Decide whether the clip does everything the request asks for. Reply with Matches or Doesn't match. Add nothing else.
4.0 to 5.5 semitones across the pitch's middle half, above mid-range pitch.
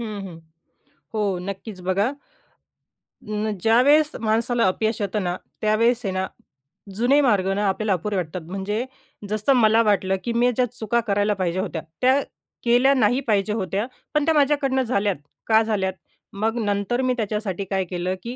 Doesn't match